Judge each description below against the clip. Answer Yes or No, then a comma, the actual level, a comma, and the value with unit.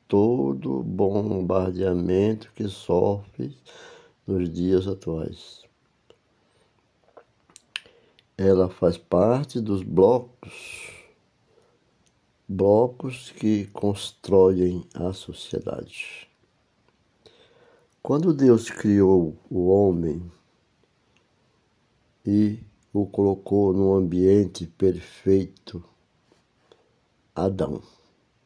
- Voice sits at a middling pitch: No, low, 100 Hz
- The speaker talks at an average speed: No, slow, 60 wpm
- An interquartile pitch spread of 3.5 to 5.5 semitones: No, narrow, 2.6 semitones